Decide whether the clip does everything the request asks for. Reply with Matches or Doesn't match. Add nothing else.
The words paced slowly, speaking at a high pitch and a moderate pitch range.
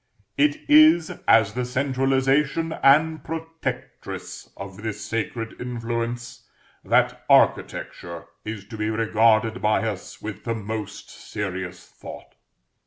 Doesn't match